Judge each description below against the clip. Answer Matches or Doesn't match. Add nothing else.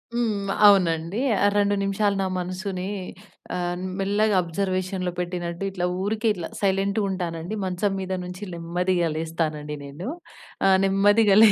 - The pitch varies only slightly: Matches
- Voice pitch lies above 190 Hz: Doesn't match